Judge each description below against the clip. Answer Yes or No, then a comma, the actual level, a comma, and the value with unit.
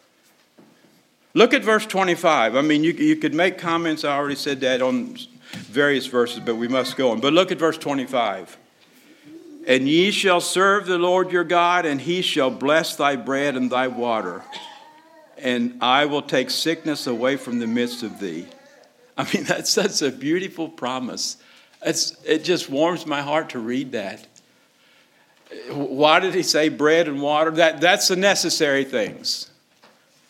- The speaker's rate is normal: Yes, average, 165 wpm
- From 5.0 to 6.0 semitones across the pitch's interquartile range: Yes, wide, 5.5 semitones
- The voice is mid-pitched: Yes, medium, 160 Hz